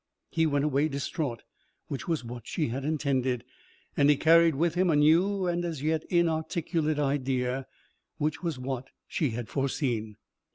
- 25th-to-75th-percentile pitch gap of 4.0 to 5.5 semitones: No, average, 3.6 semitones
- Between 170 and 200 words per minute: No, average, 160 wpm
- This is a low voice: No, medium, 150 Hz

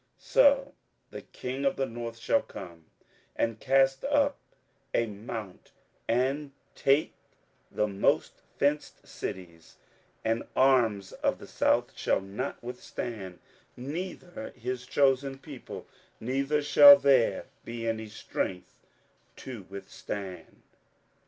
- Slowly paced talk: Yes, slow, 115 wpm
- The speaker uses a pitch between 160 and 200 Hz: No, low, 125 Hz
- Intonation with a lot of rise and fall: No, average, 4.7 semitones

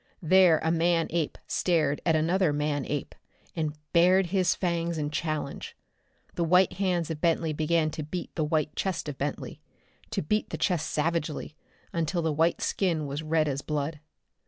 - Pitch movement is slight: Yes, narrow, 2.3 semitones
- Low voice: No, medium, 160 Hz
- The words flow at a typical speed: Yes, average, 170 wpm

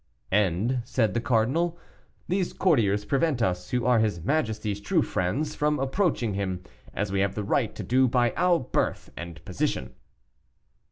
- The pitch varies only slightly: No, wide, 5.6 semitones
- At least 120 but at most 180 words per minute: Yes, average, 160 wpm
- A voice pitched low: Yes, low, 115 Hz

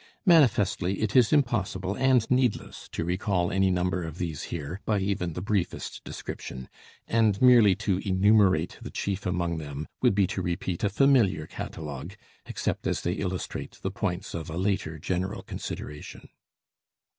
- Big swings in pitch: No, average, 3.2 semitones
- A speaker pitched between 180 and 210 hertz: No, very low, 95 Hz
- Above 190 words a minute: No, average, 155 wpm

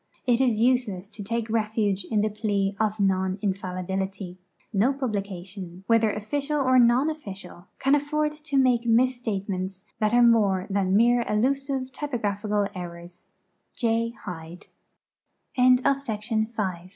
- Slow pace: Yes, slow, 120 wpm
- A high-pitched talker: Yes, high, 215 Hz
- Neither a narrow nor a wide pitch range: Yes, average, 4.2 semitones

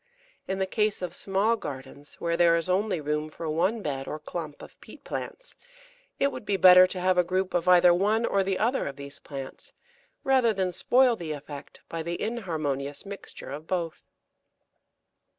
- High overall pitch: No, medium, 180 Hz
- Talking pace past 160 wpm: Yes, average, 185 wpm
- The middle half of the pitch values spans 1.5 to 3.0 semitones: No, average, 4.4 semitones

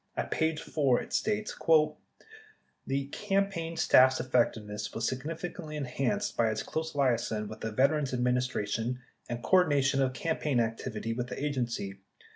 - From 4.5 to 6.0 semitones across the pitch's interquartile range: Yes, average, 5.0 semitones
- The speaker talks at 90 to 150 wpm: Yes, average, 140 wpm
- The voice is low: Yes, low, 130 Hz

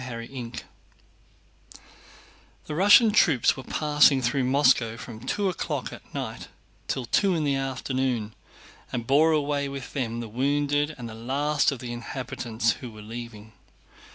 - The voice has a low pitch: Yes, low, 130 Hz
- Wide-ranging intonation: No, average, 3.7 semitones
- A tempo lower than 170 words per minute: Yes, average, 150 wpm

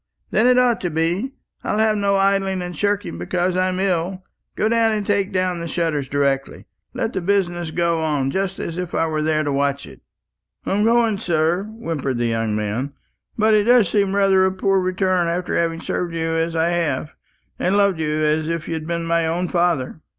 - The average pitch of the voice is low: No, medium, 175 Hz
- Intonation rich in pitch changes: No, average, 3.7 semitones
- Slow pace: No, average, 200 wpm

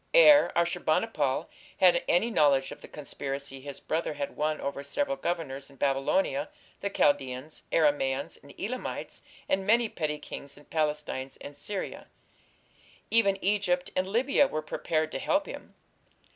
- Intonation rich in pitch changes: Yes, wide, 6.1 semitones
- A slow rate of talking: No, average, 150 wpm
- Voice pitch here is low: No, medium, 155 Hz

